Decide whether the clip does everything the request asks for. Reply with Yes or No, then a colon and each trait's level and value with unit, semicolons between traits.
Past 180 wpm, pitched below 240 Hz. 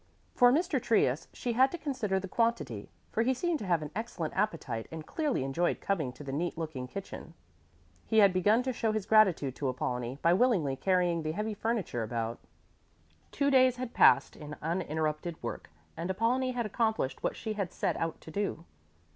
Yes: average, 190 wpm; high, 190 Hz